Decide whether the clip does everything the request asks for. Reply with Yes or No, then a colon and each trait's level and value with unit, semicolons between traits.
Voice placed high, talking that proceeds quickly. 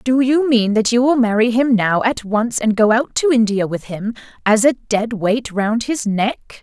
Yes: high, 230 Hz; fast, 225 wpm